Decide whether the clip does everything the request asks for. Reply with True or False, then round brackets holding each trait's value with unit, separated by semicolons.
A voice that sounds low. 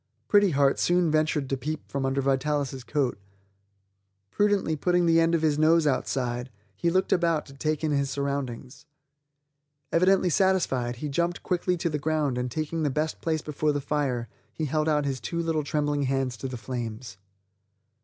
False (150 Hz)